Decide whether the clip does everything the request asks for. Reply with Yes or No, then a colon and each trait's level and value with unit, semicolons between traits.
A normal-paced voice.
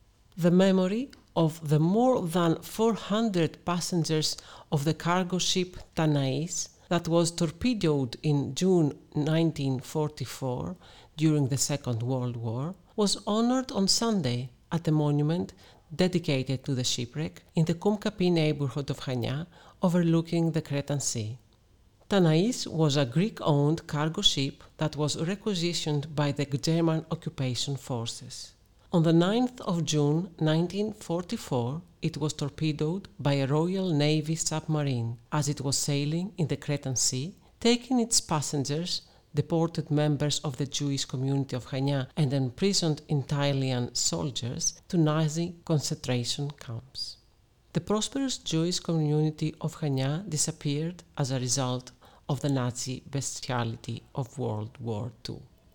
Yes: average, 130 wpm